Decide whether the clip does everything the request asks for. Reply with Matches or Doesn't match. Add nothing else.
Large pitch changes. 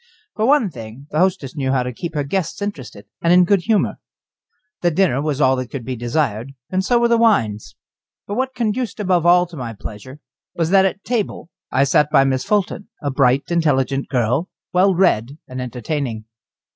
Matches